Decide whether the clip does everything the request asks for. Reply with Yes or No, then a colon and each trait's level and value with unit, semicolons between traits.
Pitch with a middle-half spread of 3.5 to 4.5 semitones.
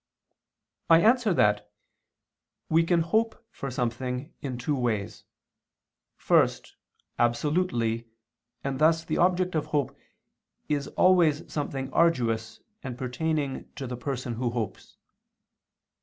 No: average, 5.3 semitones